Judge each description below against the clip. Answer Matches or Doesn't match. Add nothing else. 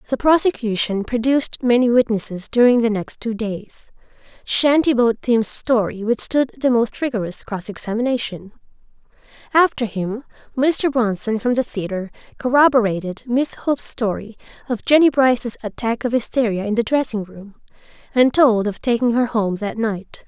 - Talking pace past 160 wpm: Doesn't match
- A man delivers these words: Doesn't match